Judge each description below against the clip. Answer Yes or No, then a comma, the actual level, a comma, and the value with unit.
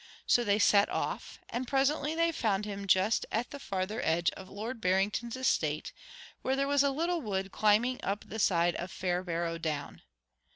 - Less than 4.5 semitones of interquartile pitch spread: No, wide, 5.6 semitones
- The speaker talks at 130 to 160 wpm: No, average, 175 wpm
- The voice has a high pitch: Yes, high, 210 Hz